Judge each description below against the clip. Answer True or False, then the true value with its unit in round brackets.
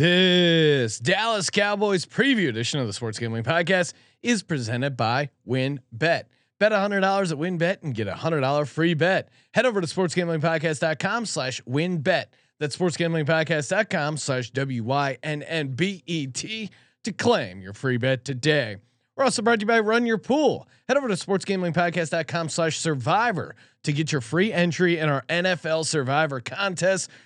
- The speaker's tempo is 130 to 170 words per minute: False (185 wpm)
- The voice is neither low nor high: True (160 Hz)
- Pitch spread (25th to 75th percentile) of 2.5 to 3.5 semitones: False (5.1 semitones)